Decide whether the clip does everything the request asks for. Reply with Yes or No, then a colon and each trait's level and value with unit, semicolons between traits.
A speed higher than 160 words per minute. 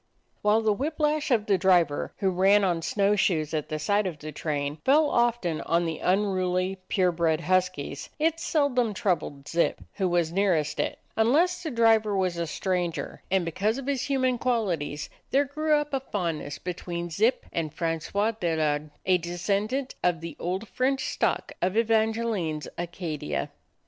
Yes: average, 175 wpm